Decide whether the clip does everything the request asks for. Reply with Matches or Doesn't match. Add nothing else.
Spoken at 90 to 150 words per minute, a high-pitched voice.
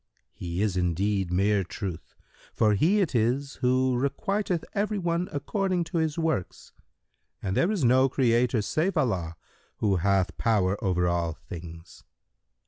Doesn't match